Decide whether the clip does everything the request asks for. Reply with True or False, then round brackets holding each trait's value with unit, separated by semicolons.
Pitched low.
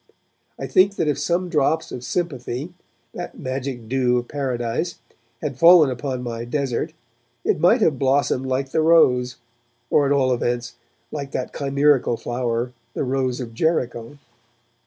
True (130 Hz)